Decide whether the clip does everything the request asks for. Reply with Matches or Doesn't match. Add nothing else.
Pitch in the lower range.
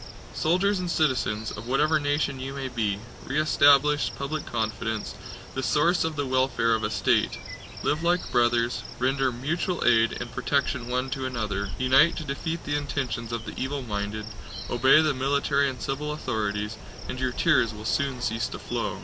Matches